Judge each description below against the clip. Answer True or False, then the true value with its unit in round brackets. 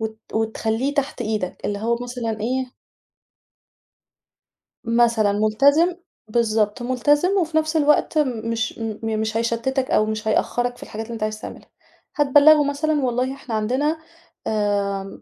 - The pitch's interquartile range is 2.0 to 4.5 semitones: True (4.1 semitones)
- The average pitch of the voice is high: True (235 Hz)